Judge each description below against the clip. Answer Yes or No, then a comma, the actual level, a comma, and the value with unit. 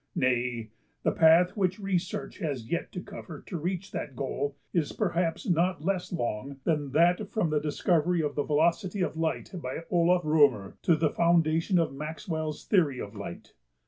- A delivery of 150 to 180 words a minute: Yes, average, 170 wpm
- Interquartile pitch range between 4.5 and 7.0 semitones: No, average, 3.6 semitones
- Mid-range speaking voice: Yes, medium, 165 Hz